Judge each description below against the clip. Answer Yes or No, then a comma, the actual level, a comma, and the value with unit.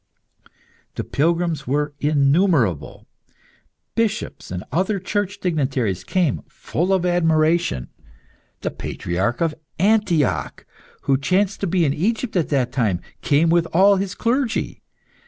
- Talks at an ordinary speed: No, slow, 120 wpm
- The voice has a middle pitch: Yes, medium, 165 Hz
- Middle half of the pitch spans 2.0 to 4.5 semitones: No, wide, 5.5 semitones